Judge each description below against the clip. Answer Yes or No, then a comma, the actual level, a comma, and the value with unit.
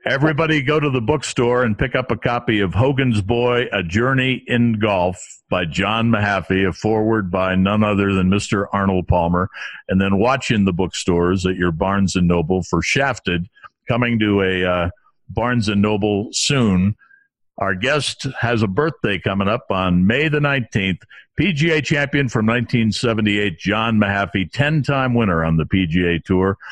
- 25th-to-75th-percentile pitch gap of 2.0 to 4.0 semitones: No, average, 4.4 semitones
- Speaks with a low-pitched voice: Yes, low, 105 Hz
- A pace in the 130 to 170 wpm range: Yes, average, 160 wpm